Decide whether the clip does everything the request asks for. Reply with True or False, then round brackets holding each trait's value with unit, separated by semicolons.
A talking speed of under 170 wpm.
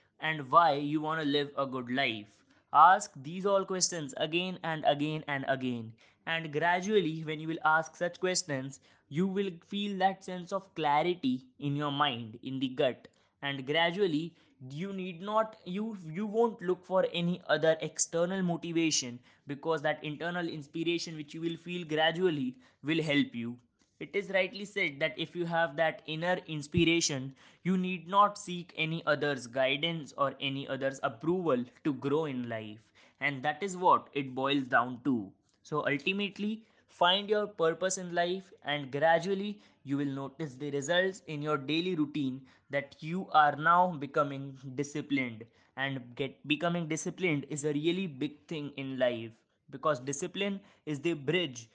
True (160 wpm)